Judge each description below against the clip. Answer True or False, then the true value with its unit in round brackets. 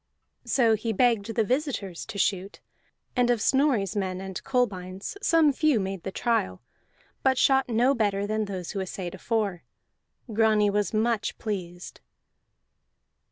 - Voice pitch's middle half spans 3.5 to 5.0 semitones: True (4.0 semitones)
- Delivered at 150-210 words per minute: False (140 wpm)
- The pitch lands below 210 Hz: False (215 Hz)